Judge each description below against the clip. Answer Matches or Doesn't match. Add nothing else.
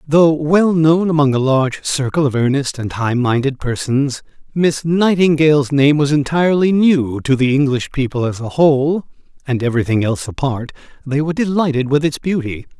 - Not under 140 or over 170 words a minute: Matches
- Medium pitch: Matches